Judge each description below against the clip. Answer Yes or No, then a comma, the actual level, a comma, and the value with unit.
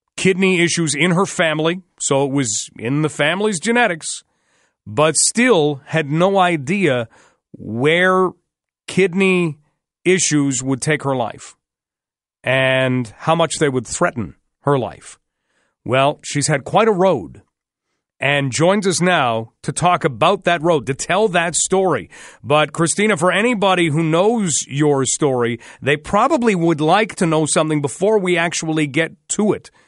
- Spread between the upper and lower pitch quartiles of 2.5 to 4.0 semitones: No, average, 4.6 semitones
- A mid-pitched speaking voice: Yes, medium, 160 Hz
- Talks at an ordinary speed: Yes, average, 145 wpm